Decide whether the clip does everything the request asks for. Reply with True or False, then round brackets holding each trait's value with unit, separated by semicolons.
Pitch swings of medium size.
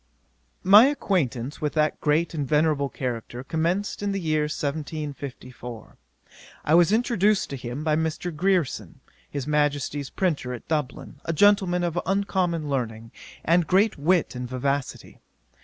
True (4.3 semitones)